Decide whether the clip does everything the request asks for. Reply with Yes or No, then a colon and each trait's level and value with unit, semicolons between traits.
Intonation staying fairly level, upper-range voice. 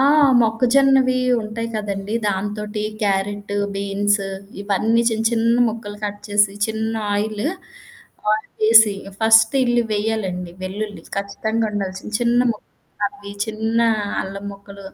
Yes: narrow, 1.9 semitones; high, 210 Hz